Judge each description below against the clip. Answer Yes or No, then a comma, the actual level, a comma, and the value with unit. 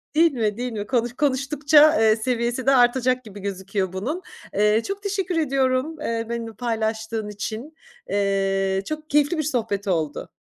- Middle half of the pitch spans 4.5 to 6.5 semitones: Yes, average, 5.3 semitones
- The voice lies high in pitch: Yes, high, 235 Hz